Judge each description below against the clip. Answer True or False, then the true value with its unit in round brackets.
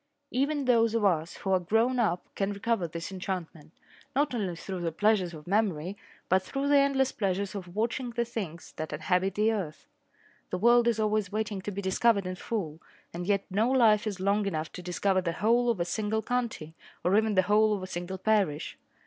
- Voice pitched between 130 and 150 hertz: False (200 Hz)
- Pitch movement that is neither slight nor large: True (3.9 semitones)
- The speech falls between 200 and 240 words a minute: True (205 wpm)